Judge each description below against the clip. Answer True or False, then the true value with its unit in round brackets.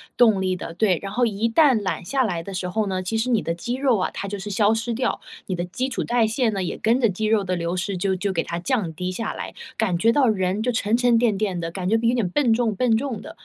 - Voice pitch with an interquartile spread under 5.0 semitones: True (4.0 semitones)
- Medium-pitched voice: False (210 Hz)